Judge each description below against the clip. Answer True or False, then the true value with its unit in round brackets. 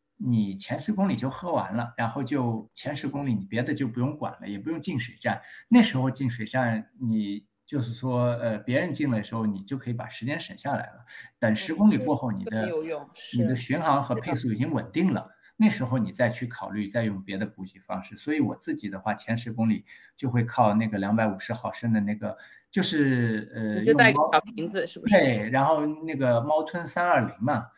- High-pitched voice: False (120 Hz)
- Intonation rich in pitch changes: False (4.3 semitones)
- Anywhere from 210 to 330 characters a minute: True (305 characters per minute)